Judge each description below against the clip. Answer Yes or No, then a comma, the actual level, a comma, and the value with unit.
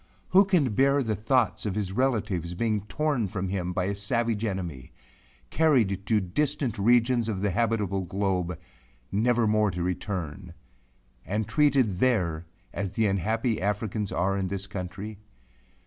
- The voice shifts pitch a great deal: No, average, 3.7 semitones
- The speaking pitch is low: Yes, low, 105 Hz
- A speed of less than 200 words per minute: Yes, average, 150 wpm